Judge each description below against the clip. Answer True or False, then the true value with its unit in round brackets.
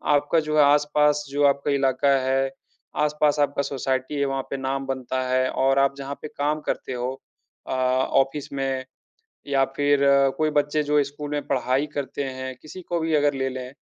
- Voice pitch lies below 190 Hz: True (140 Hz)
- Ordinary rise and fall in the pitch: False (1.8 semitones)